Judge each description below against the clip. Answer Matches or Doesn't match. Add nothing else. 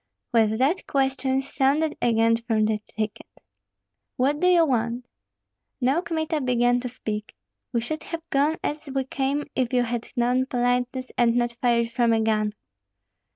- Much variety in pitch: Doesn't match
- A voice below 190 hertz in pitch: Doesn't match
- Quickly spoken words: Doesn't match